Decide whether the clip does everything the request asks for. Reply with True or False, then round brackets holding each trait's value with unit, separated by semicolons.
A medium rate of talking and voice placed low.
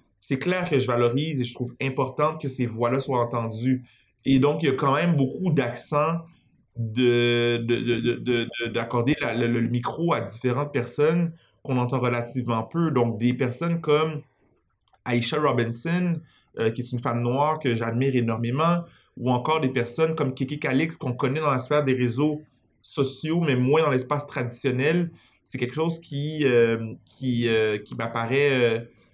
True (175 wpm; 130 Hz)